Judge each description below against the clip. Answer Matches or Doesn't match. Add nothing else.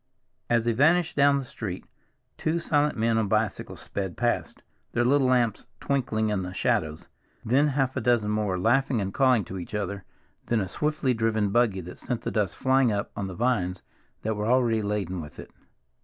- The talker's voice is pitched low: Matches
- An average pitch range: Matches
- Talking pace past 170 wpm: Matches